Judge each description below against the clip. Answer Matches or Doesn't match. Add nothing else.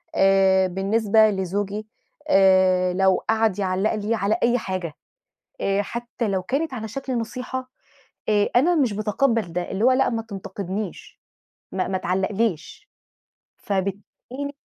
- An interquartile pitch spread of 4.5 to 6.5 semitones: Doesn't match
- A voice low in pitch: Doesn't match